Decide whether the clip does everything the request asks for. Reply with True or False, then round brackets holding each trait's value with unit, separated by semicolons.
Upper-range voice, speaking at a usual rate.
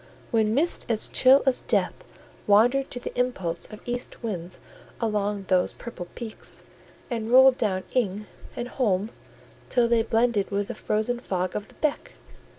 True (225 Hz; 155 wpm)